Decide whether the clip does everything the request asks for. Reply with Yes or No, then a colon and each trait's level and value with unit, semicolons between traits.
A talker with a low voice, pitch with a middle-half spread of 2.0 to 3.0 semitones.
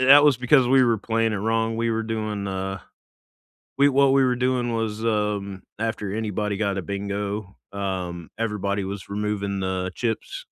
Yes: low, 105 Hz; narrow, 2.5 semitones